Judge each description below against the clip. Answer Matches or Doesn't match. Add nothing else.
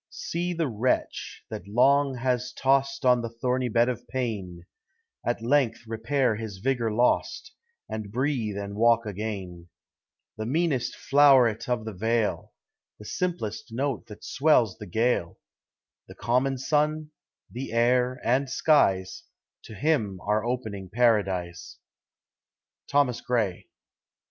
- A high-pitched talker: Doesn't match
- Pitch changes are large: Doesn't match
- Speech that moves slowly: Matches